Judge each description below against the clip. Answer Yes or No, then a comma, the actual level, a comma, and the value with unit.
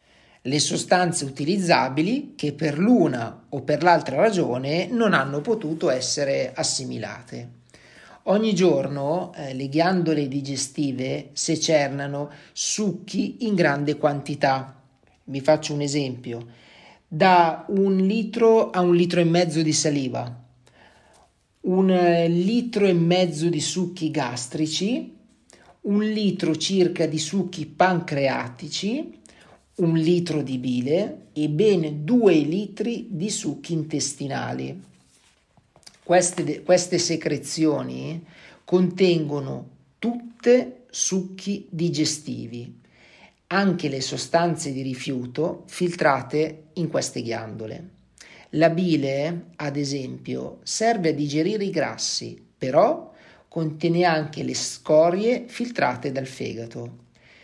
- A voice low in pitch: No, medium, 155 Hz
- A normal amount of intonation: Yes, average, 4.6 semitones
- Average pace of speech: No, slow, 105 wpm